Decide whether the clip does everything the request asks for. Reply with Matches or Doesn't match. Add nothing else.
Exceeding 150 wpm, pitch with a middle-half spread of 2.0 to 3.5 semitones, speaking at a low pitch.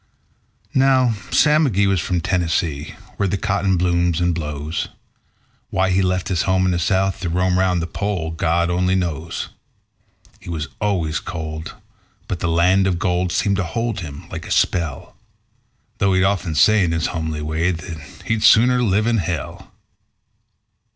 Matches